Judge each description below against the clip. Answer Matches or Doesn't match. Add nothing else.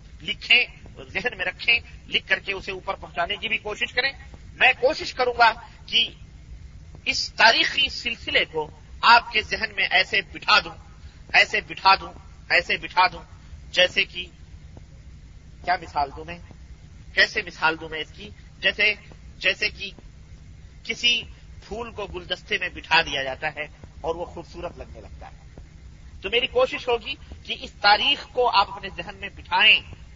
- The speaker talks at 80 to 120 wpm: Doesn't match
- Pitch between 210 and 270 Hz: Doesn't match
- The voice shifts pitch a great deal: Matches